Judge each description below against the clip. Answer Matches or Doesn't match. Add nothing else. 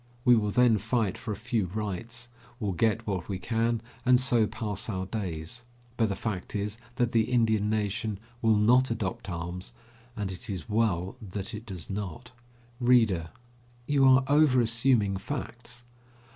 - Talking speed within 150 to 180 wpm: Matches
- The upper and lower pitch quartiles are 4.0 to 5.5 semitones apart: Doesn't match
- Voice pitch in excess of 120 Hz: Doesn't match